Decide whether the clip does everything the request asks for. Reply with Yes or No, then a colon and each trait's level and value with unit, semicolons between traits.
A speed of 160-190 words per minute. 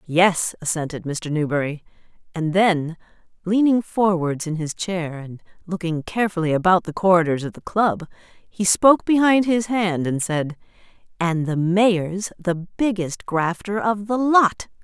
No: average, 145 wpm